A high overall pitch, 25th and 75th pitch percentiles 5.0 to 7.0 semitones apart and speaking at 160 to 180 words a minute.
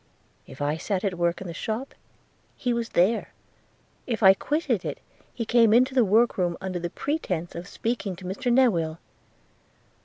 Yes: high, 200 Hz; average, 5.3 semitones; average, 175 wpm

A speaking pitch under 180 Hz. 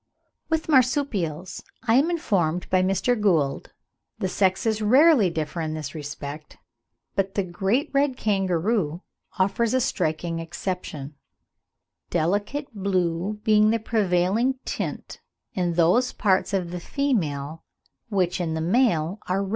No: high, 190 Hz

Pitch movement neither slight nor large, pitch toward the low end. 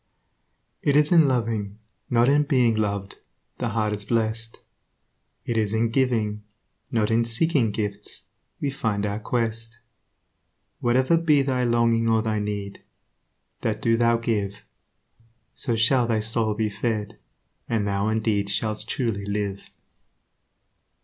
No: narrow, 2.2 semitones; low, 115 Hz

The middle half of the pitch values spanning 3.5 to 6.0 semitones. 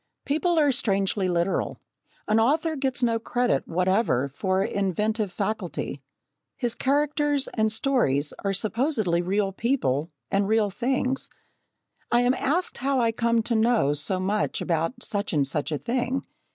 Yes: wide, 5.4 semitones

